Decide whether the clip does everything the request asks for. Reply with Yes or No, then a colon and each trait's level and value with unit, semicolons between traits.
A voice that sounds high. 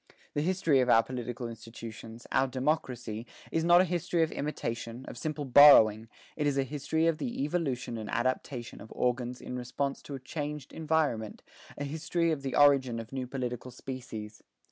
No: low, 130 Hz